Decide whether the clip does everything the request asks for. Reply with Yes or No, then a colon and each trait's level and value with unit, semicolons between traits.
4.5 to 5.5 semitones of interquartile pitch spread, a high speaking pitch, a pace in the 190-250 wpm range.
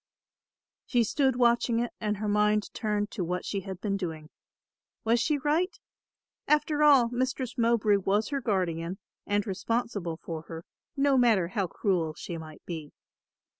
No: average, 5.0 semitones; high, 210 Hz; average, 155 wpm